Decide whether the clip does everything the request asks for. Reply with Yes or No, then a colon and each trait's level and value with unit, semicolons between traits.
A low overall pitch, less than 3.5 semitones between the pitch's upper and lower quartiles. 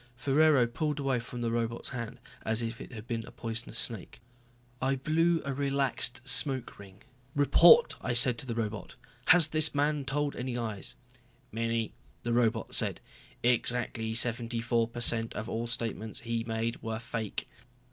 Yes: low, 120 Hz; average, 2.9 semitones